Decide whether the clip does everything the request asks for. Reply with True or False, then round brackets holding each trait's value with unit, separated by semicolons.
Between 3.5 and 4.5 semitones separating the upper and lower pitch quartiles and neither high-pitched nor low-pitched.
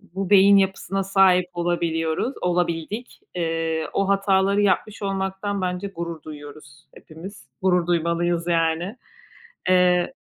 False (2.7 semitones; 180 Hz)